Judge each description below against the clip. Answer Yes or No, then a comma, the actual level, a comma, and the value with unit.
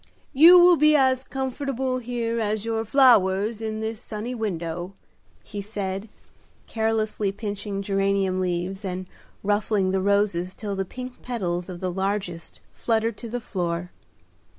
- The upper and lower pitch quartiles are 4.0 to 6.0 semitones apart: No, average, 3.4 semitones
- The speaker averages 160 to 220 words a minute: No, average, 140 wpm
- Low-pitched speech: No, high, 210 Hz